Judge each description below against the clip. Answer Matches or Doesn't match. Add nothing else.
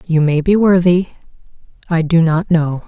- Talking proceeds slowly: Doesn't match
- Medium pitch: Matches